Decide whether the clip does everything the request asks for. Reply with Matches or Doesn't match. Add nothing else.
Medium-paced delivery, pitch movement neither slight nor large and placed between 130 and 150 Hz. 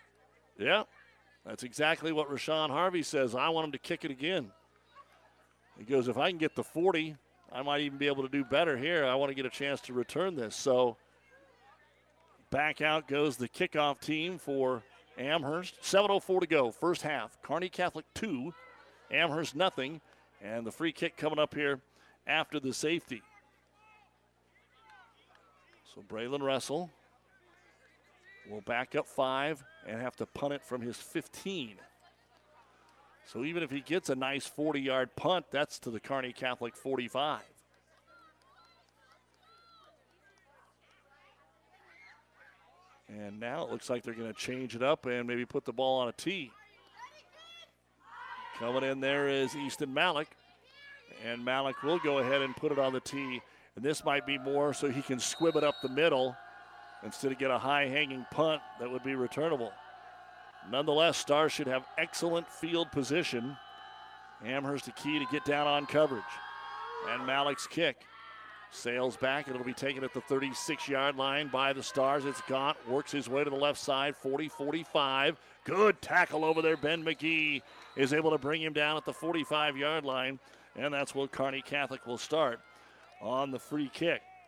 Matches